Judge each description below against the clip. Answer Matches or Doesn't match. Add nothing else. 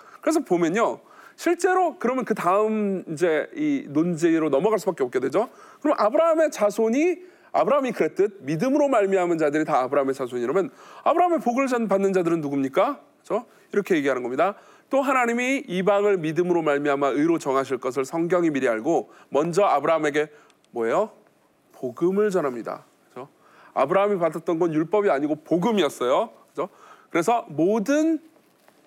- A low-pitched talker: Doesn't match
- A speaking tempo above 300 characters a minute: Matches